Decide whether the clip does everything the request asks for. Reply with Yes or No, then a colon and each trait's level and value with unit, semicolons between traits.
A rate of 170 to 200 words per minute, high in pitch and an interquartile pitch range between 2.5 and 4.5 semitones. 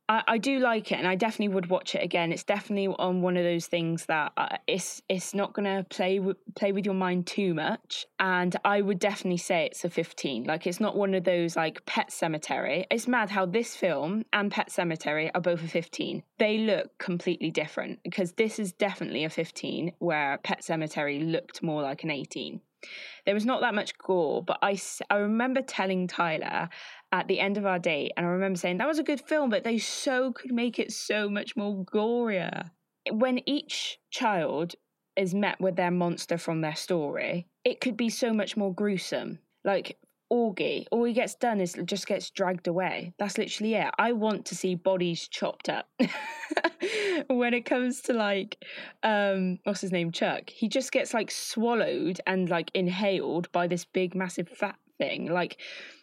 Yes: average, 195 wpm; high, 195 Hz; average, 4.0 semitones